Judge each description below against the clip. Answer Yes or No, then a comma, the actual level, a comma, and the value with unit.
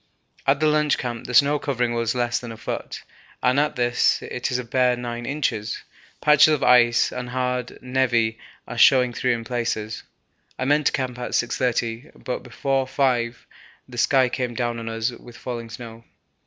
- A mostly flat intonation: Yes, narrow, 1.8 semitones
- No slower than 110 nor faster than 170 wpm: No, average, 180 wpm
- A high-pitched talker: No, low, 125 Hz